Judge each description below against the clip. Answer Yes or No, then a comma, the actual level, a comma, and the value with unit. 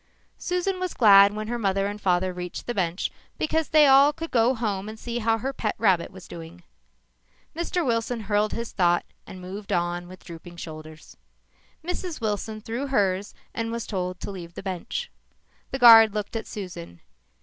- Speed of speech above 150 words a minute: Yes, average, 185 wpm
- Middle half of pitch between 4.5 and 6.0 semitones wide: Yes, average, 4.8 semitones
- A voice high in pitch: Yes, high, 210 Hz